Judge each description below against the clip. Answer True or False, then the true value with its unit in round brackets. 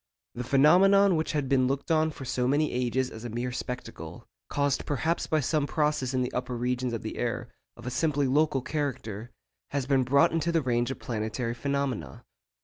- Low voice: True (130 Hz)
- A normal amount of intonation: True (3.4 semitones)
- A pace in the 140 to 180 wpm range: False (195 wpm)